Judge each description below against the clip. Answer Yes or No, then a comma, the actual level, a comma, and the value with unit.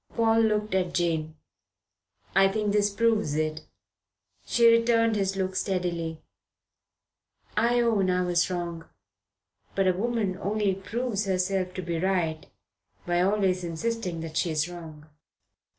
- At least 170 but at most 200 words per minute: No, slow, 135 wpm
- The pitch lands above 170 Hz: Yes, high, 190 Hz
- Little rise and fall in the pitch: No, average, 3.5 semitones